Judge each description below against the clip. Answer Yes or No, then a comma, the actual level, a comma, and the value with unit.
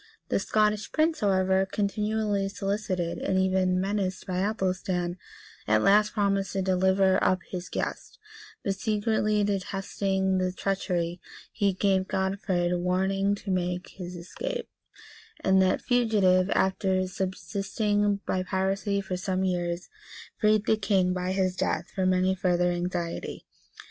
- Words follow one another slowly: Yes, slow, 130 wpm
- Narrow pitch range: Yes, narrow, 1.6 semitones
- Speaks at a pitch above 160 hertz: Yes, high, 190 Hz